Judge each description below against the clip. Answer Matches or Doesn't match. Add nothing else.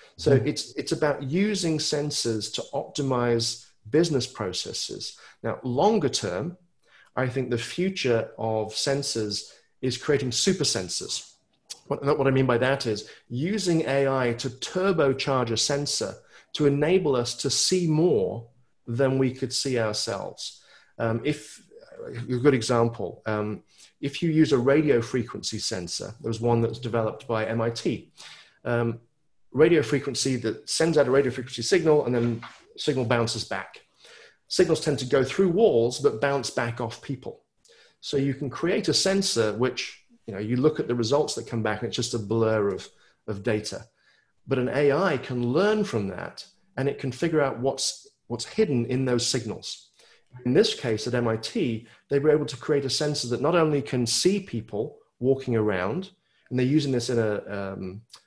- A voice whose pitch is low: Matches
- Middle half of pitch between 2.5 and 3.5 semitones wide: Doesn't match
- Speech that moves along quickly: Doesn't match